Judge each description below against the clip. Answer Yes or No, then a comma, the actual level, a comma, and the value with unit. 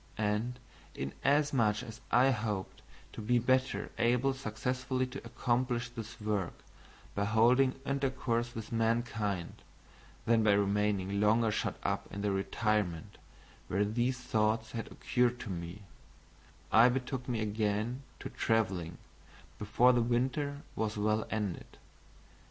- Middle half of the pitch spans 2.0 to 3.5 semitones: Yes, average, 3.0 semitones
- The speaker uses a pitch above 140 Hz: No, low, 115 Hz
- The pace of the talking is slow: Yes, slow, 125 wpm